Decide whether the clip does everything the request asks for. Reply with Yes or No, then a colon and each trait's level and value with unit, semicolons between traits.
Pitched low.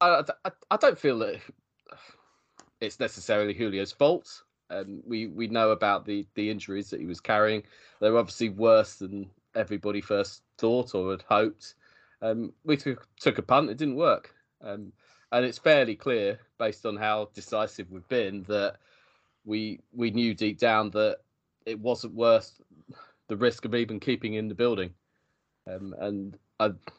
Yes: low, 110 Hz